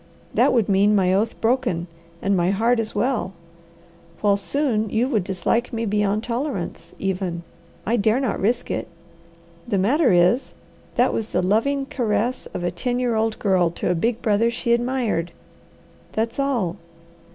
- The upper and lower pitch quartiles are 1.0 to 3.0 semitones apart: No, average, 3.9 semitones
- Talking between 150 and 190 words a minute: Yes, average, 165 wpm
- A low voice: No, high, 220 Hz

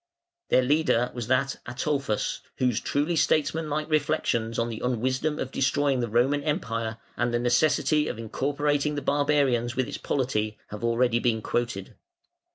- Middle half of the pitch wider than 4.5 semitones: No, average, 3.6 semitones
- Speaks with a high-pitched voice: No, low, 130 Hz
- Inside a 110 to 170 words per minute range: Yes, average, 150 wpm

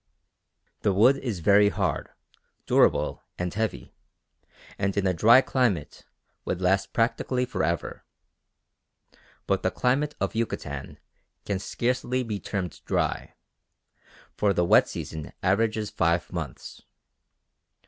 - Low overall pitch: Yes, low, 100 Hz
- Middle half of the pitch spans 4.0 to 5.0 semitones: Yes, average, 4.6 semitones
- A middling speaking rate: No, slow, 115 wpm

